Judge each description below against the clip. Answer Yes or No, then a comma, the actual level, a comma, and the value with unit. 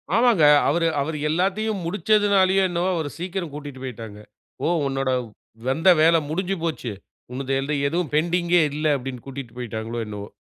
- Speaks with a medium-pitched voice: Yes, medium, 160 Hz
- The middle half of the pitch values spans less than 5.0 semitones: No, wide, 5.4 semitones